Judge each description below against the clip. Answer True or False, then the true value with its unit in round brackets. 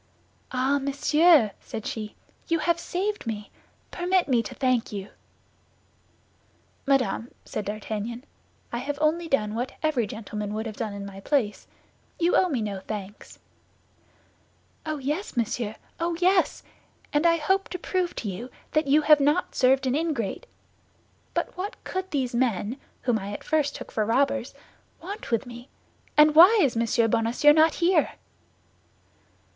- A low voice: False (265 Hz)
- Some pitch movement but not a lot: False (6.2 semitones)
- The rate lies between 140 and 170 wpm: True (150 wpm)